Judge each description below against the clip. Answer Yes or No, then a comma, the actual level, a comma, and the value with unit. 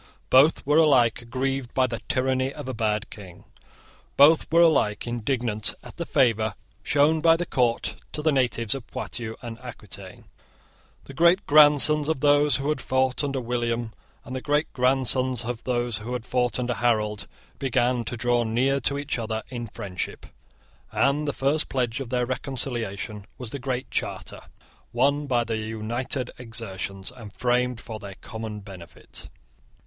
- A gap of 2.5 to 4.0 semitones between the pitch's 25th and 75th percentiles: Yes, average, 3.2 semitones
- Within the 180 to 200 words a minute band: No, average, 165 wpm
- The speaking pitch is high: No, low, 125 Hz